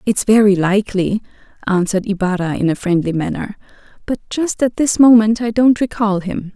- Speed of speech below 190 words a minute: Yes, average, 165 wpm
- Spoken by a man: No, female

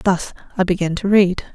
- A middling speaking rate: Yes, average, 195 wpm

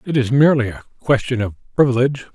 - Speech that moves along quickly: No, average, 180 wpm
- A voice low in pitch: Yes, low, 125 Hz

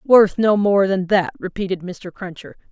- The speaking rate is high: No, average, 175 wpm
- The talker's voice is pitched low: No, high, 190 Hz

